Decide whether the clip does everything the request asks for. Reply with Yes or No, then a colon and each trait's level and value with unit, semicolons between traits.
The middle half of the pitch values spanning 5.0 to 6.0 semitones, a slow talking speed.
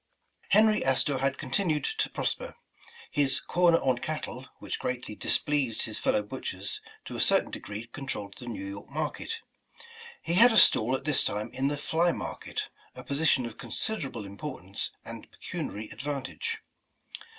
No: wide, 5.6 semitones; average, 165 wpm